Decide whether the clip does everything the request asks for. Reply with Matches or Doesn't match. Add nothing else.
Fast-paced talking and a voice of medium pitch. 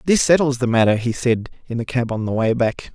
Doesn't match